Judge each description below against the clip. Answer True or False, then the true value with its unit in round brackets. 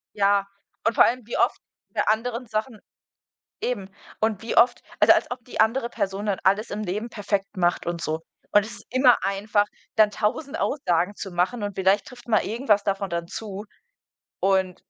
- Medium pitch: False (210 Hz)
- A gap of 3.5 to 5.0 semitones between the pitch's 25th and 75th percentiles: False (3.0 semitones)